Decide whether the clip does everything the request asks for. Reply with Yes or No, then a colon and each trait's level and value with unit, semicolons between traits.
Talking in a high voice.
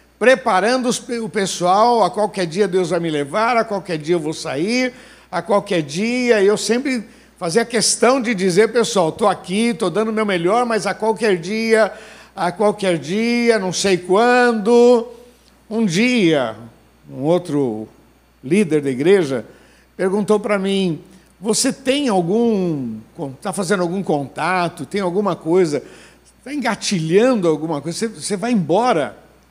Yes: high, 205 Hz